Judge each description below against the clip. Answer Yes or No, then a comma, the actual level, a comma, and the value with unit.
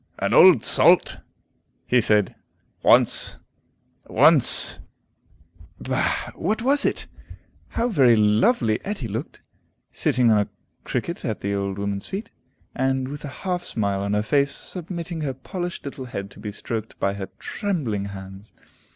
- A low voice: Yes, low, 120 Hz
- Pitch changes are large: Yes, wide, 8.5 semitones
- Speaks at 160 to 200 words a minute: No, average, 145 wpm